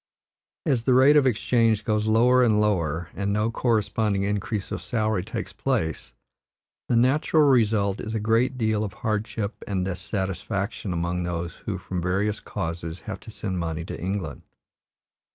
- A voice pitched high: No, low, 105 Hz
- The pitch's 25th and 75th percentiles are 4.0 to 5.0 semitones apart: No, average, 3.6 semitones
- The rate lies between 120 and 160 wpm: Yes, average, 155 wpm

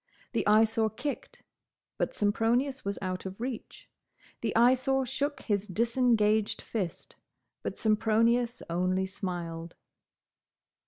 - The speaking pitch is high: Yes, high, 220 Hz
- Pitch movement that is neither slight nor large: Yes, average, 4.2 semitones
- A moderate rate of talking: No, slow, 105 wpm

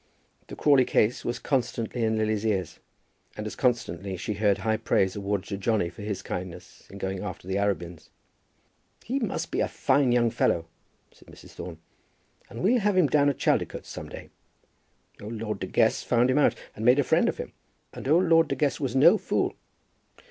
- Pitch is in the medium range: No, low, 110 Hz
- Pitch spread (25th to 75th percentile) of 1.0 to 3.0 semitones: No, average, 5.1 semitones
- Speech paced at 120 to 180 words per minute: No, average, 195 wpm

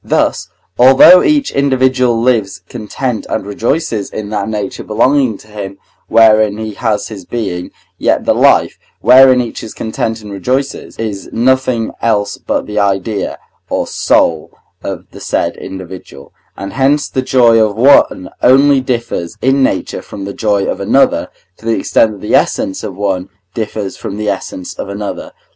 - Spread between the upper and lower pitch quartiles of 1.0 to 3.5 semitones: No, average, 4.1 semitones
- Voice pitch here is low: Yes, low, 110 Hz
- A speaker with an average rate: Yes, average, 160 wpm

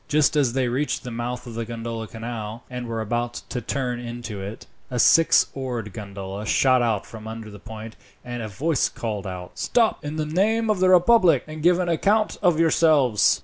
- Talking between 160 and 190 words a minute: No, average, 200 wpm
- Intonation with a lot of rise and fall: Yes, wide, 5.7 semitones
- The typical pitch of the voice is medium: No, low, 120 Hz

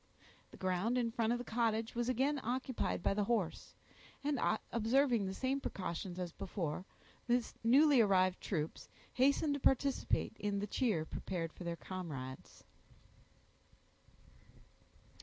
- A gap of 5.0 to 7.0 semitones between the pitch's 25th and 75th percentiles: Yes, wide, 5.5 semitones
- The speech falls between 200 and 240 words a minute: No, slow, 135 wpm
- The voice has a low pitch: No, high, 225 Hz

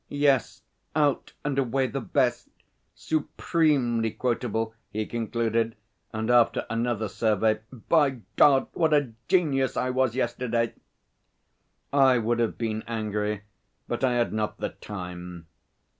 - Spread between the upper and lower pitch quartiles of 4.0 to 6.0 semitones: No, average, 3.3 semitones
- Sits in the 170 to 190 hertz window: No, low, 120 Hz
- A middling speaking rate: No, slow, 125 wpm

